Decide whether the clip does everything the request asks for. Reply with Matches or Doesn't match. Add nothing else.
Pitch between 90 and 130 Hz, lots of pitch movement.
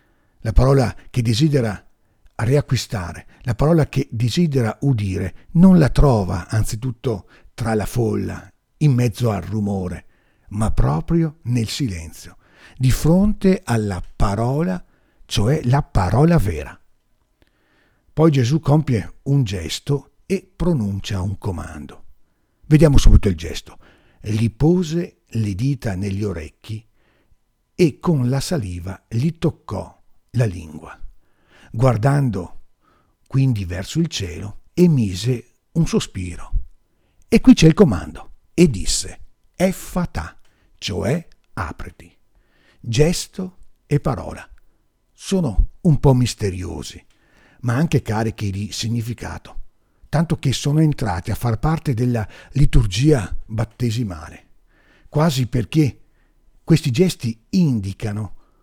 Matches